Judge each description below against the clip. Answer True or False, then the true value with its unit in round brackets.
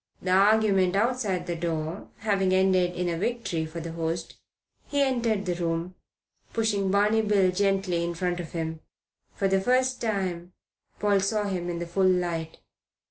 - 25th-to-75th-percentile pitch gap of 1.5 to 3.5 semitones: True (3.1 semitones)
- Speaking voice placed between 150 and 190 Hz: True (185 Hz)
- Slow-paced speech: False (165 wpm)